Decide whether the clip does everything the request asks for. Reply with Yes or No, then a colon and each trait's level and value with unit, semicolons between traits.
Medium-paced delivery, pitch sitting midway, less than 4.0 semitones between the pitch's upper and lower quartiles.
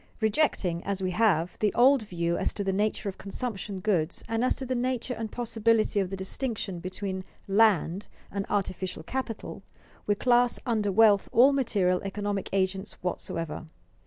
No: average, 160 wpm; high, 205 Hz; average, 3.4 semitones